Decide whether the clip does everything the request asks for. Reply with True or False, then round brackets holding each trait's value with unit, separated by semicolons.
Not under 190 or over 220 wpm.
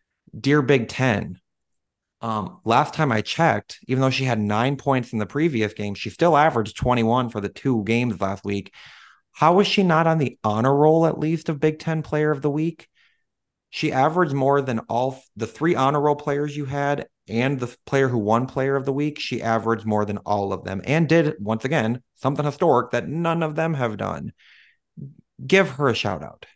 True (205 wpm)